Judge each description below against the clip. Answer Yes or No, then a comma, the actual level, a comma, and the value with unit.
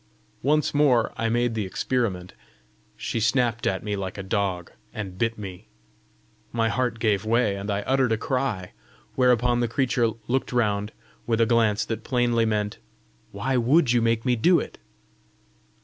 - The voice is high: No, low, 115 Hz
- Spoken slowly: No, average, 165 wpm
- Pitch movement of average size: Yes, average, 3.1 semitones